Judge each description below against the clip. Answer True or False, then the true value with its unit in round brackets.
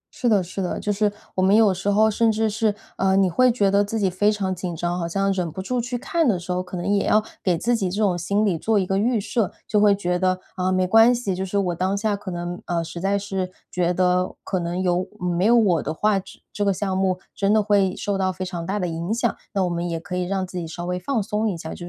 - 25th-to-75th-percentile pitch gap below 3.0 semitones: True (2.6 semitones)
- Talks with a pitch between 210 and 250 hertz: False (190 Hz)